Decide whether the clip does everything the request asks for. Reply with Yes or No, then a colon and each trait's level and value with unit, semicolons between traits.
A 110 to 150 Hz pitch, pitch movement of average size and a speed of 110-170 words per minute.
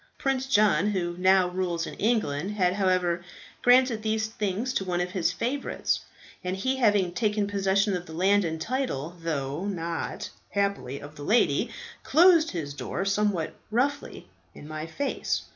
No: high, 195 Hz; average, 4.0 semitones; average, 160 wpm